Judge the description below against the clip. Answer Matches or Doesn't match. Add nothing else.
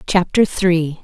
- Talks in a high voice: Doesn't match